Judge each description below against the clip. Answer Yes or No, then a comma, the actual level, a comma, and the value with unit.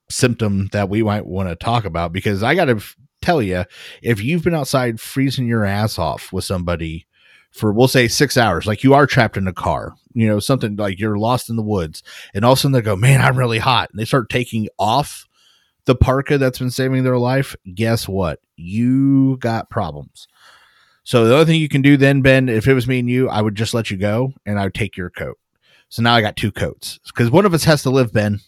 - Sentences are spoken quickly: Yes, fast, 240 wpm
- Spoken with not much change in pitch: No, average, 4.1 semitones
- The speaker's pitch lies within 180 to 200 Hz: No, low, 115 Hz